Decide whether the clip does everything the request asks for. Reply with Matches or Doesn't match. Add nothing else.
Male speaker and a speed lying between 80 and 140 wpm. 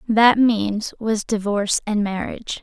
Doesn't match